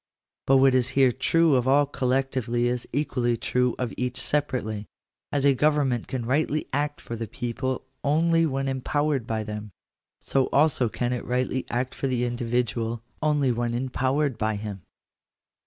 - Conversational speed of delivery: Yes, average, 160 wpm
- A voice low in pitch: Yes, low, 130 Hz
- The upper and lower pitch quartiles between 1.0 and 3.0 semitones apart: Yes, average, 2.7 semitones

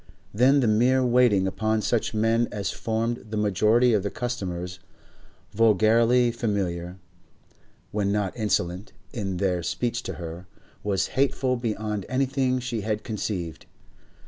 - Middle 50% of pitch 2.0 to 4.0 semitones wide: Yes, average, 3.6 semitones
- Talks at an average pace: No, slow, 130 wpm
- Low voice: Yes, low, 110 Hz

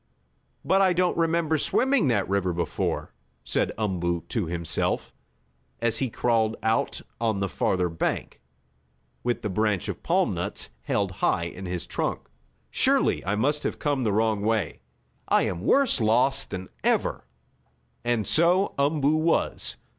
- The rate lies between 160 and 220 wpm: No, average, 145 wpm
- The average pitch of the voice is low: Yes, low, 110 Hz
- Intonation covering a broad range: Yes, wide, 7.5 semitones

